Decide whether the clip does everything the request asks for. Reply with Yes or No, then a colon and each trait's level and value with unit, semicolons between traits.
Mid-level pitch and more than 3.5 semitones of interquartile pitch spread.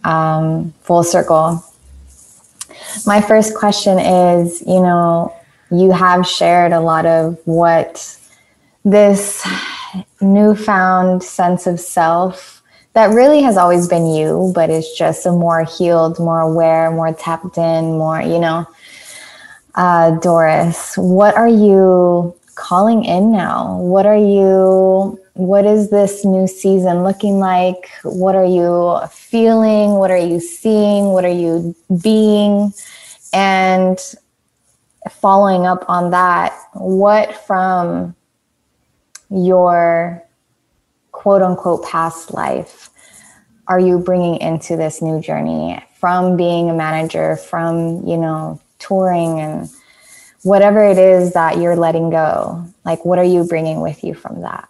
No: medium, 180 Hz; average, 2.9 semitones